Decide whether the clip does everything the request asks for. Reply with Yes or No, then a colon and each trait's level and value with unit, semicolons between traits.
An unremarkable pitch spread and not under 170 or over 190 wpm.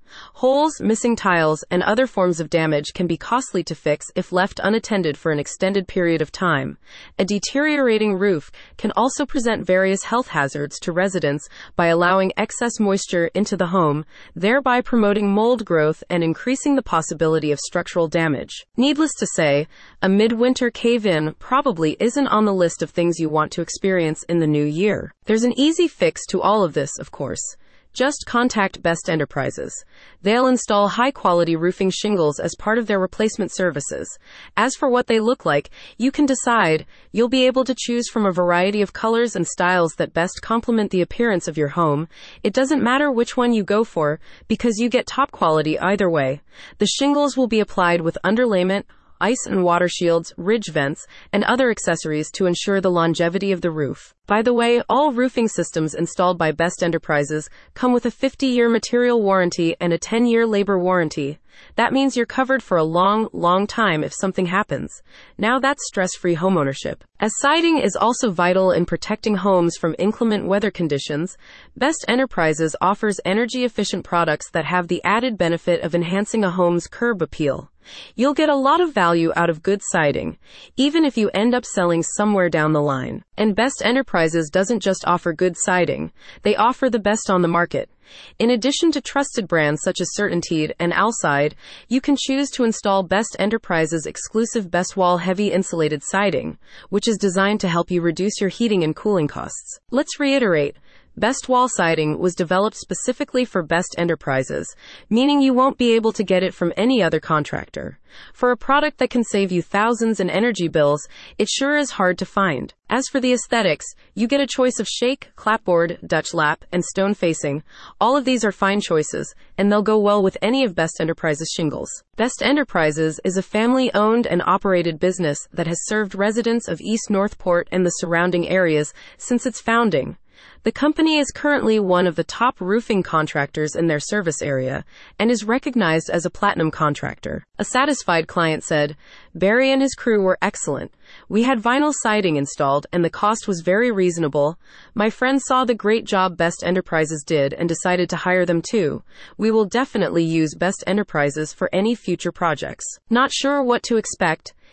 No: wide, 5.7 semitones; average, 185 wpm